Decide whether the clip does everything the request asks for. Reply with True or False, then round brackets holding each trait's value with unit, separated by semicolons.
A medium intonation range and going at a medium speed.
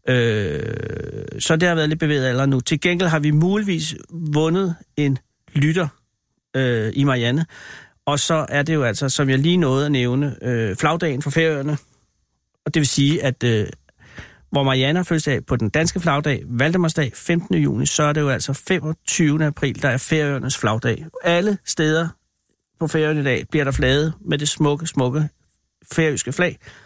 True (3.5 semitones; 175 wpm)